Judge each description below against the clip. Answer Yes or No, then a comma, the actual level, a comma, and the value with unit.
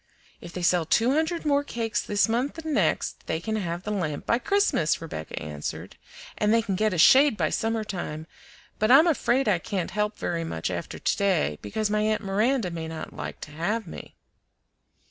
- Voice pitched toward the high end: Yes, high, 210 Hz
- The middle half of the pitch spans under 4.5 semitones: No, wide, 5.5 semitones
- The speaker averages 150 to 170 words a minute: No, average, 200 wpm